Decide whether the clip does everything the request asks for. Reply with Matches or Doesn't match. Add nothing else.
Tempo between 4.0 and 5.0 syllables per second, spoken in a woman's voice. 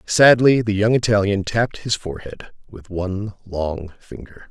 Doesn't match